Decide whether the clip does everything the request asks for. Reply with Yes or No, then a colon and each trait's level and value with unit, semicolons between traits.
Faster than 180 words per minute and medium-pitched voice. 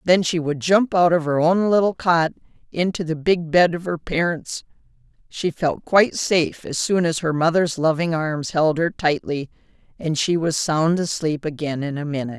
Yes: average, 195 wpm; medium, 165 Hz